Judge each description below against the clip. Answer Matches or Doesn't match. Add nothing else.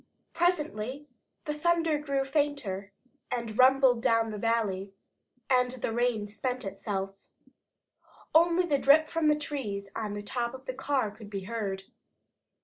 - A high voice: Matches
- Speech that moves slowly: Doesn't match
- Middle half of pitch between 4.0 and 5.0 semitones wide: Doesn't match